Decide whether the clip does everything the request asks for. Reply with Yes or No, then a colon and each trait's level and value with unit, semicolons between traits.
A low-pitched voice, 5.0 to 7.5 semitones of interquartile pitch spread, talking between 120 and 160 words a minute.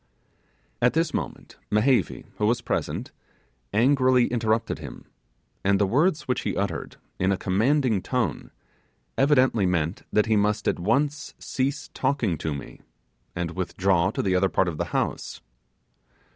Yes: low, 110 Hz; wide, 5.6 semitones; average, 145 wpm